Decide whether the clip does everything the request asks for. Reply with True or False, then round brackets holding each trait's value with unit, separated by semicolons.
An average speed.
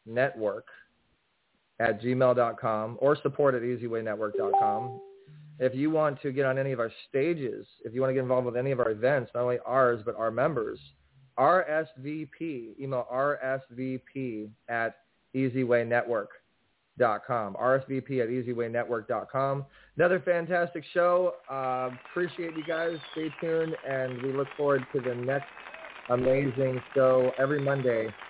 False (130 wpm)